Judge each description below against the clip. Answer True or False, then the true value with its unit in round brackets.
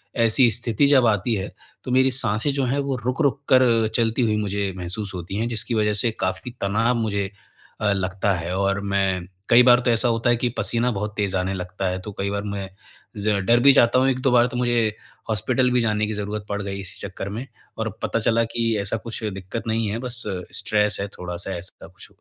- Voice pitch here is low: True (110 Hz)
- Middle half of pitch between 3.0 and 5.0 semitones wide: True (3.5 semitones)